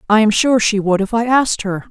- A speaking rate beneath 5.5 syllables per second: No, 5.9 syllables/s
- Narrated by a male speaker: No, female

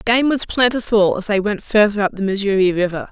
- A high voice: Yes, high, 210 Hz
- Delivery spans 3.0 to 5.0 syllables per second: No, 5.7 syllables/s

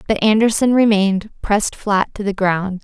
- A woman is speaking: Yes, female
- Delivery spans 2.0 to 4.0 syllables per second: No, 5.1 syllables/s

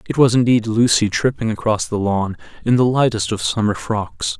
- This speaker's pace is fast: No, average, 190 wpm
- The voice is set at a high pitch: No, low, 110 Hz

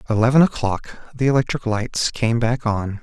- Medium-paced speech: Yes, average, 180 wpm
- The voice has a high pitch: No, low, 115 Hz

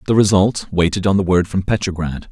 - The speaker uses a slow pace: No, fast, 205 wpm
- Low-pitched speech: Yes, very low, 95 Hz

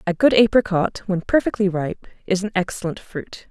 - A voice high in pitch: Yes, high, 195 Hz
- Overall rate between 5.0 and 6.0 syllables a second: Yes, 5.2 syllables/s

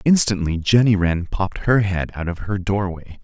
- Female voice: No, male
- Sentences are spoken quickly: No, average, 185 wpm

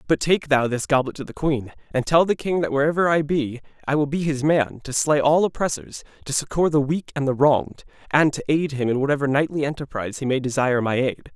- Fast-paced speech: Yes, fast, 240 wpm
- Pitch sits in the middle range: Yes, medium, 145 Hz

